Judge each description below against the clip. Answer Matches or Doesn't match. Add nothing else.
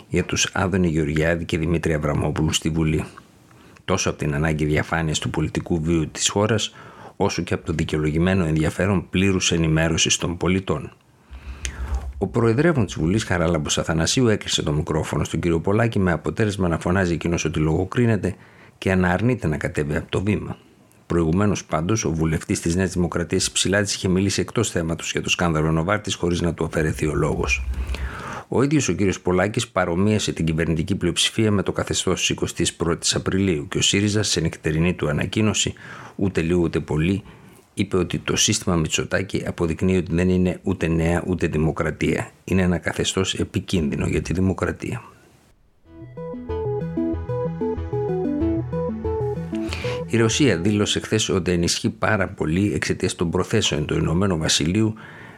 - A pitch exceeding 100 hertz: Doesn't match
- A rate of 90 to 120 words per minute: Doesn't match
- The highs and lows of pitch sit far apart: Doesn't match